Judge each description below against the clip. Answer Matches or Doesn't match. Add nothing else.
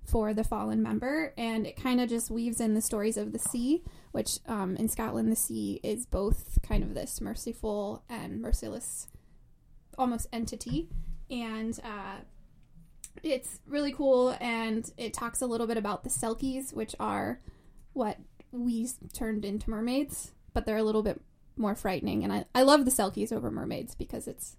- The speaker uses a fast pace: Doesn't match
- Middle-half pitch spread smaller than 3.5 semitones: Matches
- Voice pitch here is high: Matches